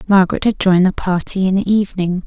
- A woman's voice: Yes, female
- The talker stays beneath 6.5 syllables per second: No, 6.6 syllables/s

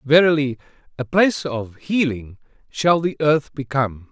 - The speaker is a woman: No, male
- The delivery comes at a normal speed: No, slow, 130 wpm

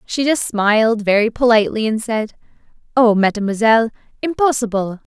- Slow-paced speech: Yes, slow, 115 wpm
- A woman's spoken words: Yes, female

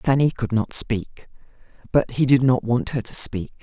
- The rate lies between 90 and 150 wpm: No, average, 200 wpm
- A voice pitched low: Yes, low, 120 Hz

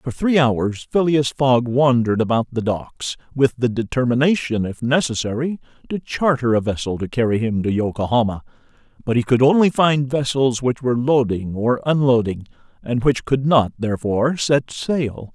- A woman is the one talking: No, male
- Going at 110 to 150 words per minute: No, average, 160 wpm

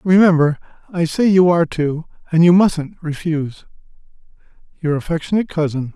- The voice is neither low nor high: Yes, medium, 165 Hz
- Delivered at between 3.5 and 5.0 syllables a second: No, 5.6 syllables/s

